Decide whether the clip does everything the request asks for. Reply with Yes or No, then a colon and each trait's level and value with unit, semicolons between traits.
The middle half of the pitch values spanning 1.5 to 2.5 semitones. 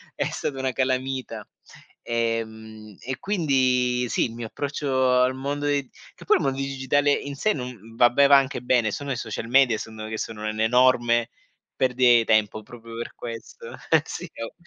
No: average, 2.9 semitones